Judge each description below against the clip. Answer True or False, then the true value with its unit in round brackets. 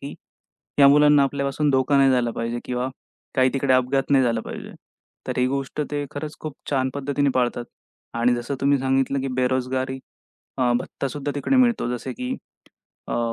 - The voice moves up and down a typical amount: False (2.0 semitones)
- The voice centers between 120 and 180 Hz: True (135 Hz)